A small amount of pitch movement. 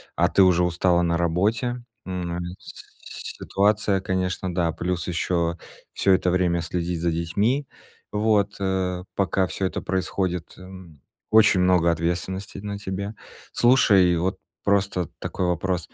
Yes: narrow, 2.2 semitones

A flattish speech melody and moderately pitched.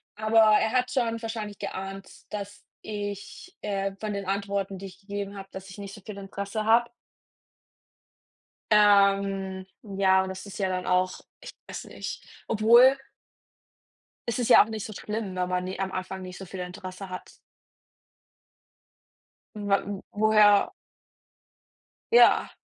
No: narrow, 2.0 semitones; high, 200 Hz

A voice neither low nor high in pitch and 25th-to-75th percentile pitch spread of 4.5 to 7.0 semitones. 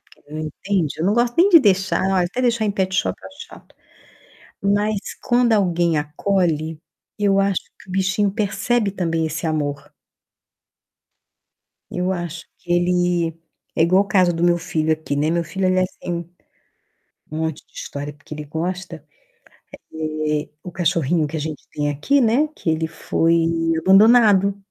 No: medium, 175 Hz; average, 3.8 semitones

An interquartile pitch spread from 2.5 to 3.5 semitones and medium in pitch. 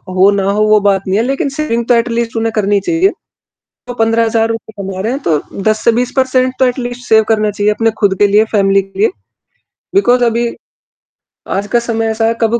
No: average, 2.9 semitones; high, 225 Hz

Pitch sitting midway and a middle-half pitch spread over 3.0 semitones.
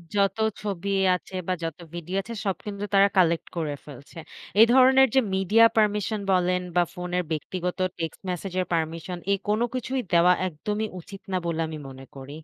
Yes: medium, 180 Hz; average, 3.5 semitones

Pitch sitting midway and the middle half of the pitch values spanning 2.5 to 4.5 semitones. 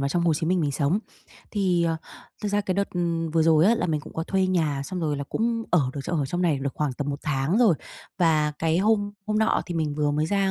Yes: medium, 165 Hz; average, 4.2 semitones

